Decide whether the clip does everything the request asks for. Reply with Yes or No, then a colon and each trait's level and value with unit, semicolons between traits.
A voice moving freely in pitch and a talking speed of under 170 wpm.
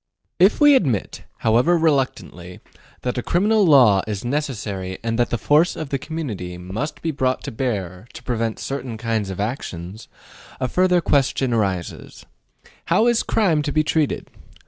Yes: wide, 6.7 semitones; average, 160 wpm